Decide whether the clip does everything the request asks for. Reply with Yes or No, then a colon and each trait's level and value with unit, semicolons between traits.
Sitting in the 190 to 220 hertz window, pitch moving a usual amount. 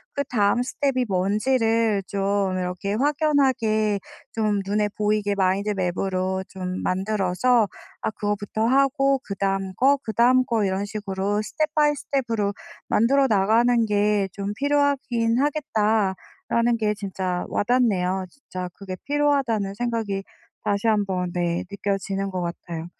Yes: high, 210 Hz; average, 3.9 semitones